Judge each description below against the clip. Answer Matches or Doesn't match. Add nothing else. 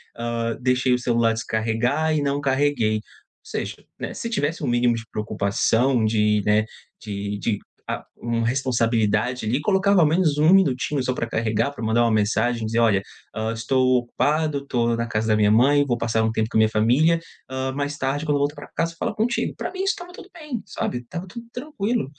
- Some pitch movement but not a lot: Matches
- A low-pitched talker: Matches